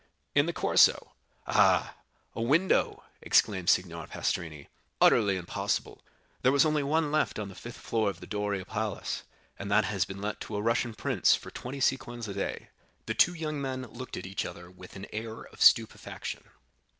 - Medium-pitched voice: No, low, 110 Hz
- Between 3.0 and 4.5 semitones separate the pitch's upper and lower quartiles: No, average, 4.9 semitones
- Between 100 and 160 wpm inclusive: No, average, 175 wpm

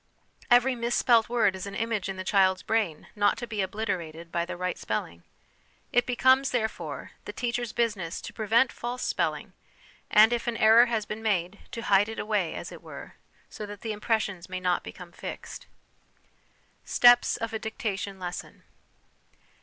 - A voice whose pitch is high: Yes, high, 215 Hz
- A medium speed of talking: Yes, average, 170 wpm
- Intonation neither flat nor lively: Yes, average, 3.9 semitones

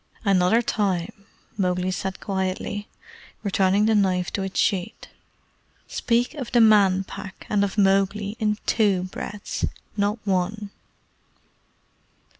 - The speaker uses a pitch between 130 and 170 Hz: No, high, 200 Hz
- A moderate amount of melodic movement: No, narrow, 2.0 semitones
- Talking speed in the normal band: No, slow, 115 wpm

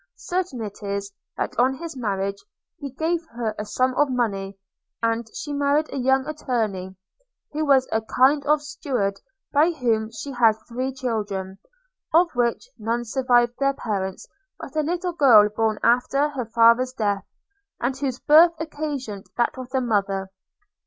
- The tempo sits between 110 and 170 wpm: Yes, average, 160 wpm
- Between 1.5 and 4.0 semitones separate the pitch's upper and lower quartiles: No, average, 4.8 semitones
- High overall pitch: Yes, very high, 250 Hz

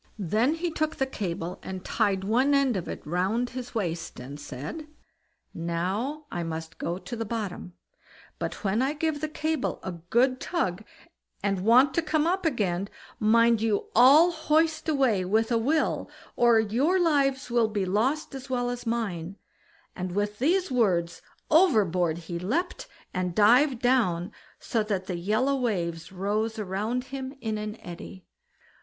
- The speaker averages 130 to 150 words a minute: No, average, 160 wpm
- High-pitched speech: Yes, high, 225 Hz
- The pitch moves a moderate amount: No, wide, 6.5 semitones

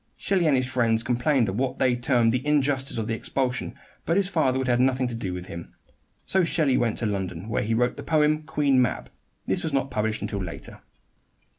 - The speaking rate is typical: No, fast, 220 wpm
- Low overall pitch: Yes, low, 125 Hz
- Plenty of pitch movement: No, average, 3.7 semitones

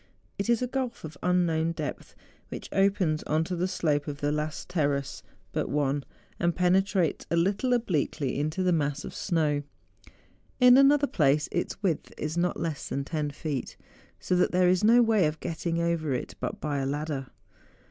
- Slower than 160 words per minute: No, average, 185 wpm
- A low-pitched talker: No, medium, 165 Hz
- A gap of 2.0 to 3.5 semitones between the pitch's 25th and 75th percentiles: No, average, 4.0 semitones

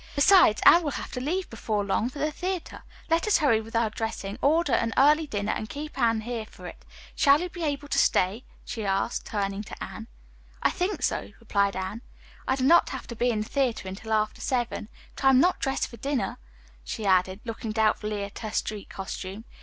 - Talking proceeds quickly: Yes, fast, 215 wpm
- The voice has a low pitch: No, high, 230 Hz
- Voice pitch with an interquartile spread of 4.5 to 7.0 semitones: Yes, average, 5.2 semitones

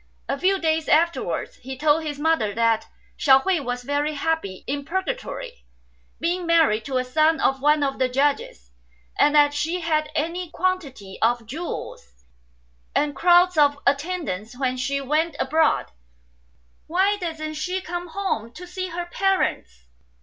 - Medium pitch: No, very high, 305 Hz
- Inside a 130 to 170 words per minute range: Yes, average, 155 wpm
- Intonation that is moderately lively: Yes, average, 4.7 semitones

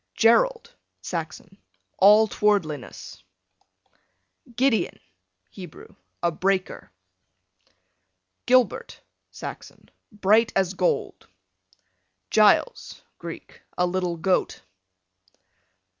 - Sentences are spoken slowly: Yes, slow, 70 wpm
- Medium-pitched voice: No, high, 195 Hz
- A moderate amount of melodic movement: Yes, average, 3.6 semitones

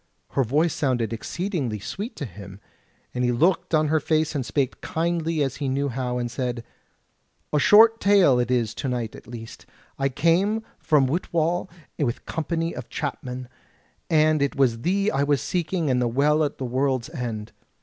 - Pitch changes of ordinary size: Yes, average, 4.9 semitones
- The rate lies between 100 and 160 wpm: No, average, 185 wpm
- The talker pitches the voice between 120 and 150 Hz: Yes, medium, 140 Hz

